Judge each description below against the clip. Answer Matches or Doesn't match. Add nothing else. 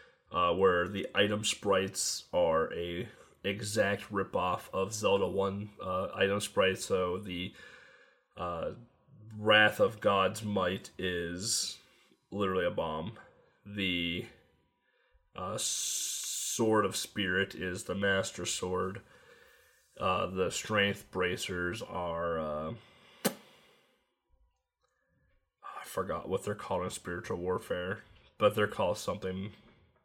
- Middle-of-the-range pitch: Doesn't match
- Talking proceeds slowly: Matches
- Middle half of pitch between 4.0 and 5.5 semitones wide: Doesn't match